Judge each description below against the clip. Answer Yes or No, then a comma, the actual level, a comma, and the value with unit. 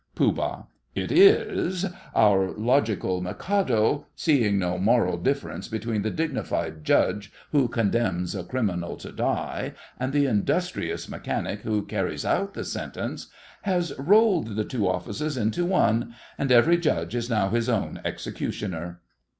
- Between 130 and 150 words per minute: Yes, slow, 135 wpm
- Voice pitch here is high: No, low, 115 Hz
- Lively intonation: Yes, wide, 6.3 semitones